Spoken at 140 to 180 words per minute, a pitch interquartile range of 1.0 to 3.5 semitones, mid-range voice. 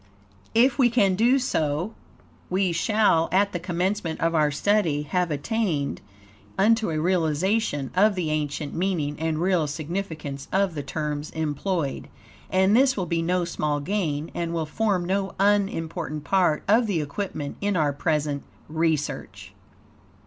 No: average, 145 wpm; average, 4.5 semitones; medium, 170 Hz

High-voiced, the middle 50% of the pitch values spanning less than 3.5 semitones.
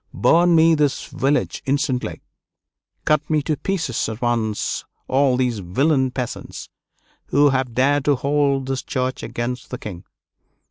No: low, 135 Hz; average, 2.8 semitones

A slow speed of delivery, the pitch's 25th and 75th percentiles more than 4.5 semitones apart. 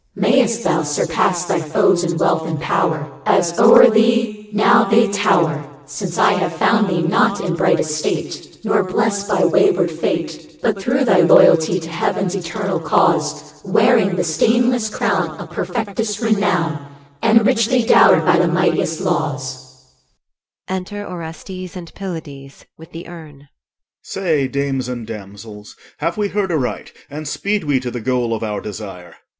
No: average, 160 wpm; wide, 5.4 semitones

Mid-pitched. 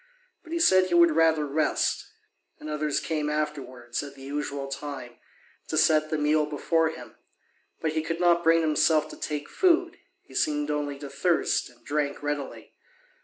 Yes: medium, 150 Hz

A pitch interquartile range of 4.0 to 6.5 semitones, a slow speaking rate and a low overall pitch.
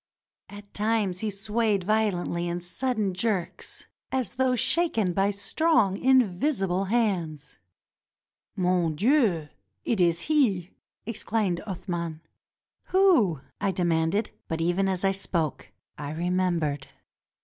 No: average, 4.3 semitones; slow, 115 wpm; high, 195 Hz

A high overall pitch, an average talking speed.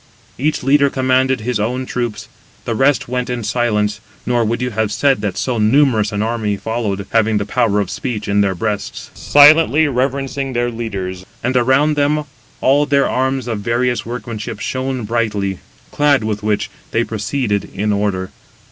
No: low, 120 Hz; average, 165 wpm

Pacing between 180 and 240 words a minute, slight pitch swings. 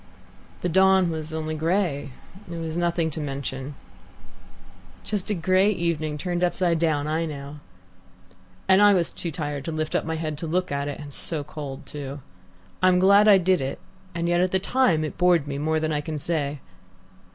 No: average, 195 wpm; average, 3.5 semitones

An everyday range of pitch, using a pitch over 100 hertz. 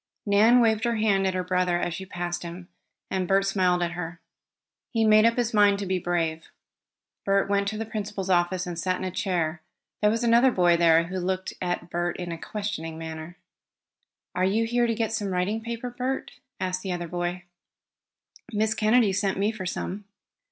Yes: average, 3.5 semitones; high, 190 Hz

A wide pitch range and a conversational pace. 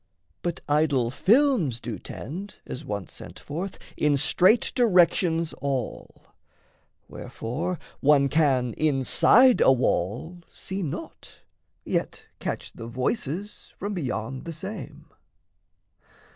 No: wide, 6.1 semitones; slow, 105 wpm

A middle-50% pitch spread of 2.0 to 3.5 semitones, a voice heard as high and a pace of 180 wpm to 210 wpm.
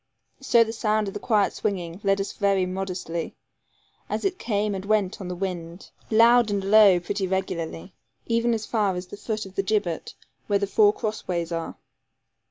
Yes: average, 2.8 semitones; high, 200 Hz; average, 185 wpm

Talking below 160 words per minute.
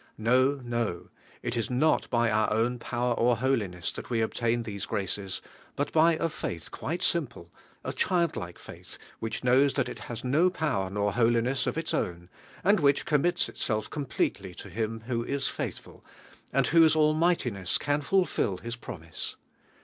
No: average, 170 wpm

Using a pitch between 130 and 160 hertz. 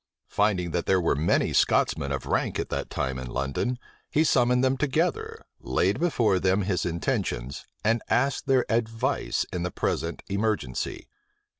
No: low, 105 Hz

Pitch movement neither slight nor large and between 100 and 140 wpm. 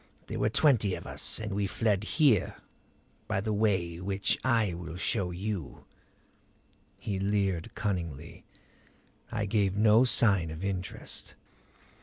Yes: average, 3.0 semitones; slow, 135 wpm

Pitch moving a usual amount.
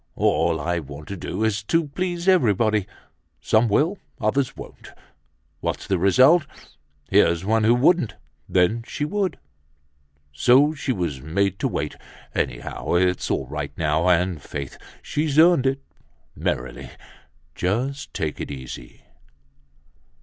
No: wide, 8.9 semitones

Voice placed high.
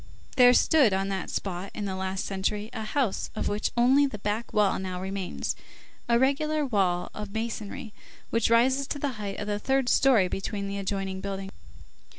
Yes: high, 210 Hz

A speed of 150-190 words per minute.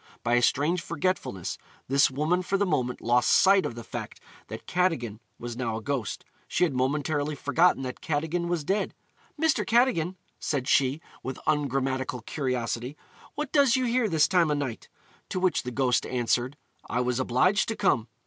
Yes: average, 175 wpm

